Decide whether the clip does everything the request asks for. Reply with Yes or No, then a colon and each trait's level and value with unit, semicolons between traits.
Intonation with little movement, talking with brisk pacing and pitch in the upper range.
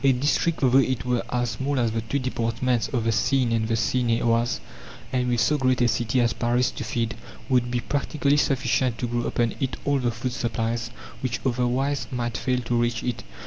No: narrow, 1.7 semitones; fast, 215 wpm; low, 120 Hz